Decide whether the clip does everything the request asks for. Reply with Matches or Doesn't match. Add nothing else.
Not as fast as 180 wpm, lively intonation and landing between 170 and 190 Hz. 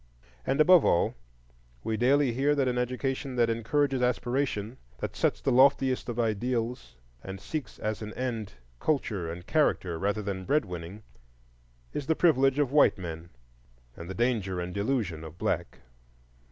Doesn't match